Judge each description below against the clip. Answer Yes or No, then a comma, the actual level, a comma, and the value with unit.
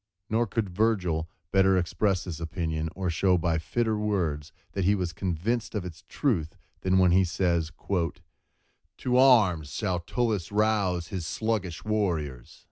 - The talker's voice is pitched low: Yes, very low, 95 Hz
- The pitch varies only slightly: No, average, 4.2 semitones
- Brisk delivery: No, average, 145 wpm